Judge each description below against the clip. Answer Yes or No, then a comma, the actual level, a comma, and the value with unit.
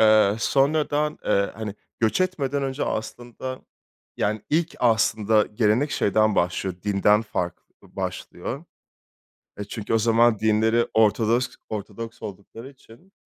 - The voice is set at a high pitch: No, low, 110 Hz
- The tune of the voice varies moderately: Yes, average, 3.5 semitones